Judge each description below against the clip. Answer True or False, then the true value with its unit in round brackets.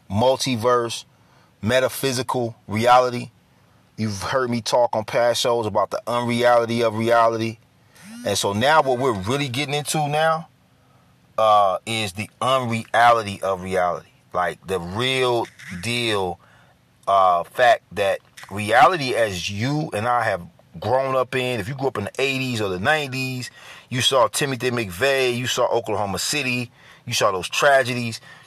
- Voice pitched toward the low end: True (120 Hz)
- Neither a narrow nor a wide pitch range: True (3.1 semitones)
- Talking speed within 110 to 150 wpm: True (145 wpm)